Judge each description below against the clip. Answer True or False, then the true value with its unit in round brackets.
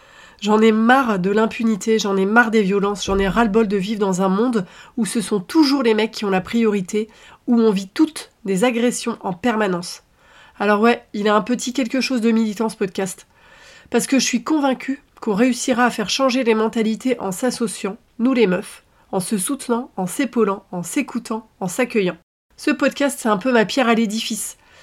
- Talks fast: False (210 wpm)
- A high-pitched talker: True (225 Hz)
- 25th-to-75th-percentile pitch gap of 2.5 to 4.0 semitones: True (3.1 semitones)